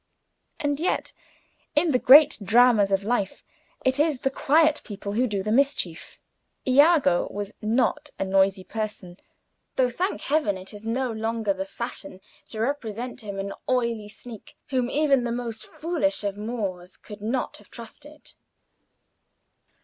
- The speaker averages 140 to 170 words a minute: Yes, average, 150 wpm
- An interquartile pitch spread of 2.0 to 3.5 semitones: No, average, 4.9 semitones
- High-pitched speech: Yes, high, 230 Hz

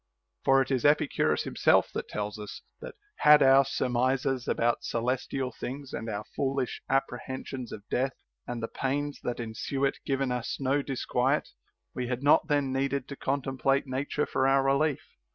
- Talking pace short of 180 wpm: Yes, average, 170 wpm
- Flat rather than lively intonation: Yes, narrow, 1.8 semitones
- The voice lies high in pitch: No, low, 135 Hz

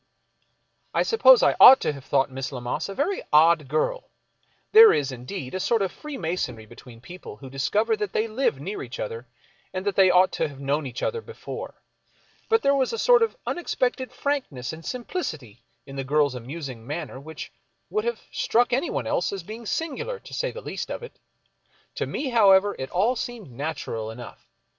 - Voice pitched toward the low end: No, medium, 180 Hz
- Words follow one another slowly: No, average, 190 wpm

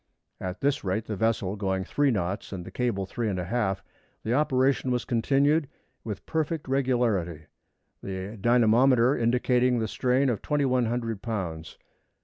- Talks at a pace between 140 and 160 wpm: Yes, average, 145 wpm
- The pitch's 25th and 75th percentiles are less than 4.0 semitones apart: No, average, 4.8 semitones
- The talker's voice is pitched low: Yes, low, 115 Hz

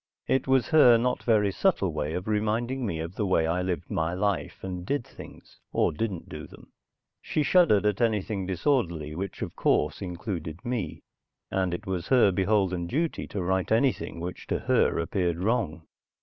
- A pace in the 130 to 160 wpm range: No, average, 180 wpm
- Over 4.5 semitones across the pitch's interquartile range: Yes, average, 4.9 semitones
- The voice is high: No, very low, 95 Hz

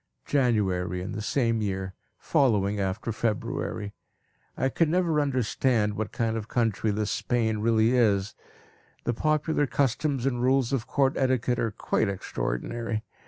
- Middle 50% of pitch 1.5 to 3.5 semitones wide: No, average, 4.0 semitones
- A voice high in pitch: No, low, 115 Hz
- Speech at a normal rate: Yes, average, 145 wpm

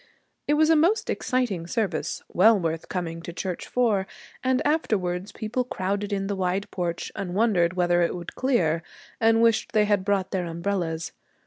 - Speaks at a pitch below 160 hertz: No, high, 195 Hz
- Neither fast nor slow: Yes, average, 175 wpm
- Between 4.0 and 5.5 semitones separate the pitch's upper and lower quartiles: Yes, average, 4.4 semitones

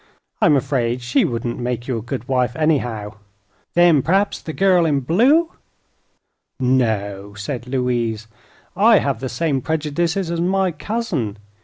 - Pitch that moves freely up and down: Yes, wide, 6.1 semitones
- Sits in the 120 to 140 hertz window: Yes, low, 135 Hz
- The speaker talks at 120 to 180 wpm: Yes, average, 145 wpm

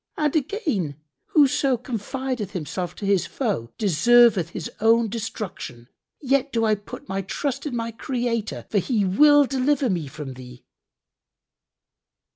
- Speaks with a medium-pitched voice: No, high, 225 Hz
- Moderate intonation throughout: No, wide, 6.2 semitones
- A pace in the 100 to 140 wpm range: Yes, slow, 135 wpm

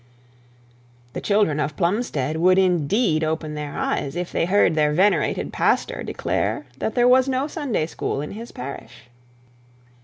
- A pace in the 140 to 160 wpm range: Yes, average, 150 wpm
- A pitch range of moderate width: No, wide, 5.7 semitones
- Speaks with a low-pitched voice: No, medium, 175 Hz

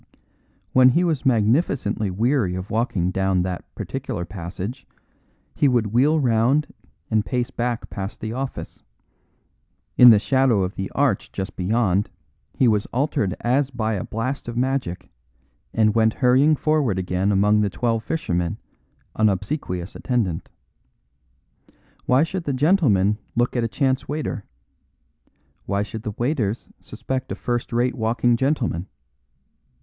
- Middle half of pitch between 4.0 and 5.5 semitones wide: Yes, average, 4.7 semitones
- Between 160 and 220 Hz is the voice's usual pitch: No, low, 115 Hz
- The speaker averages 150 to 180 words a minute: No, average, 140 wpm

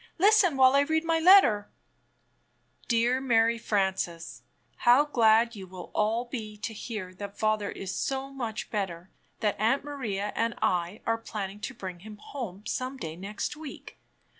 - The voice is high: Yes, high, 225 Hz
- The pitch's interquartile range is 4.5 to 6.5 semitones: Yes, average, 4.8 semitones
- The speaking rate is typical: Yes, average, 160 wpm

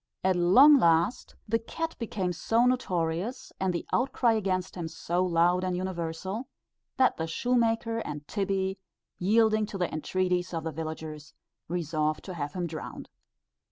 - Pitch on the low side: No, medium, 185 Hz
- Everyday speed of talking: Yes, average, 150 wpm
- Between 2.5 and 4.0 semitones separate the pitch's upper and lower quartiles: No, average, 5.1 semitones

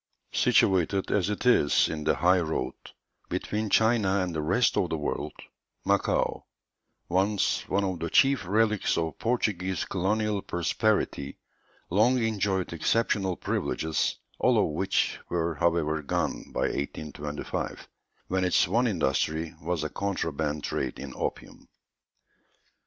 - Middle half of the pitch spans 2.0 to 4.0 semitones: No, average, 4.5 semitones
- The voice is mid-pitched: No, very low, 90 Hz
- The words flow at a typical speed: No, slow, 130 wpm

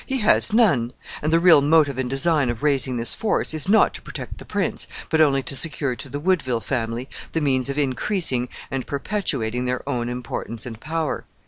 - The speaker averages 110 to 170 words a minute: No, average, 200 wpm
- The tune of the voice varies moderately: Yes, average, 4.5 semitones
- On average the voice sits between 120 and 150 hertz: Yes, medium, 140 Hz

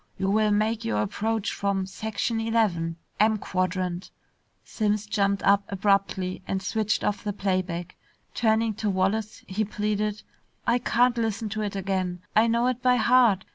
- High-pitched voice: Yes, high, 210 Hz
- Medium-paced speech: Yes, average, 160 wpm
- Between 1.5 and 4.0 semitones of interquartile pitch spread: Yes, narrow, 2.5 semitones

